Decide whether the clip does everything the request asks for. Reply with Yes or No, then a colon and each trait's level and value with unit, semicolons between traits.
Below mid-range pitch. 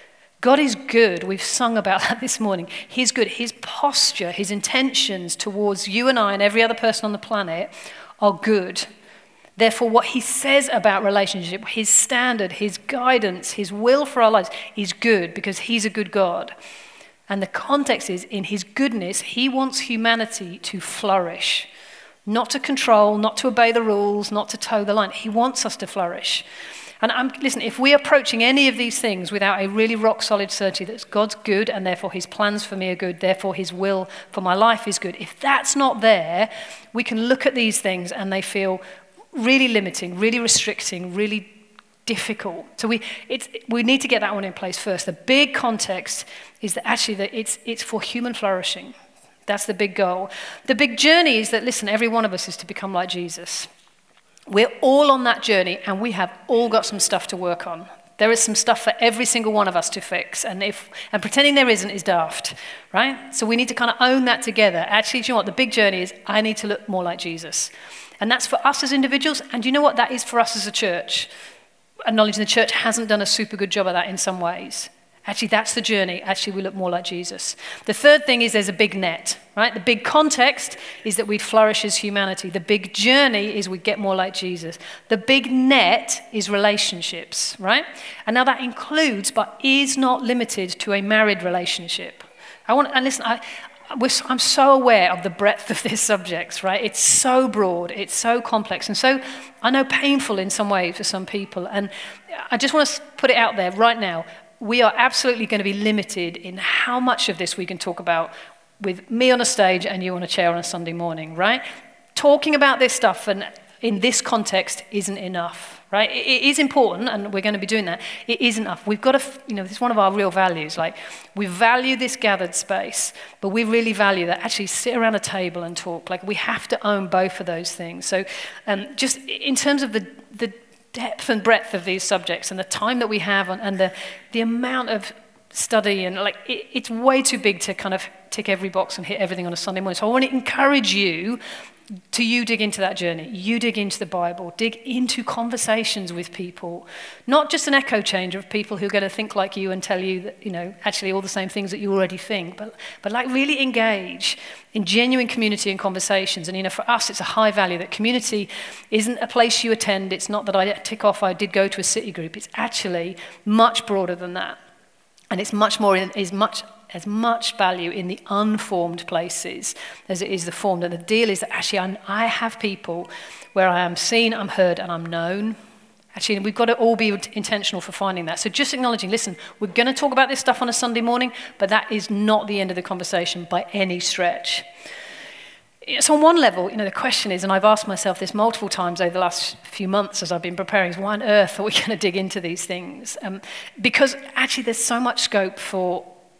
No: high, 210 Hz